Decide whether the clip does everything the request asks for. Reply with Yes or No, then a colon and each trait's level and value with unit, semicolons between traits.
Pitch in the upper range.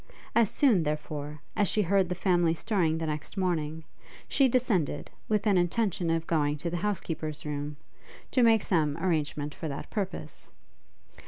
No: medium, 170 Hz